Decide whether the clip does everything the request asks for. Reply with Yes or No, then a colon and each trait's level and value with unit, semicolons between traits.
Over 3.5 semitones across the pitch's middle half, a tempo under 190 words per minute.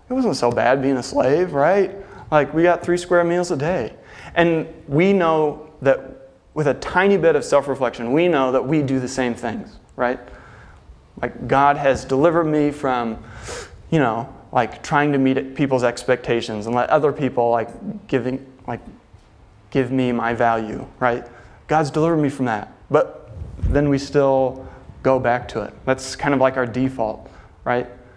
Yes: average, 3.9 semitones; average, 175 wpm